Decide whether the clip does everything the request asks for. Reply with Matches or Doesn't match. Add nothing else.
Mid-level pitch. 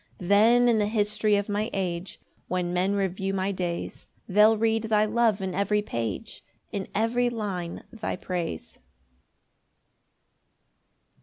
Doesn't match